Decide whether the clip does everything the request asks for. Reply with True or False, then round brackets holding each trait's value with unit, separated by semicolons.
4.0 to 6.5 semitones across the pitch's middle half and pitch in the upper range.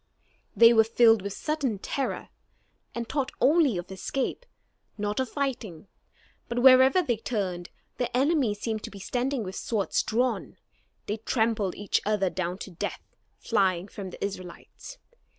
True (4.7 semitones; 225 Hz)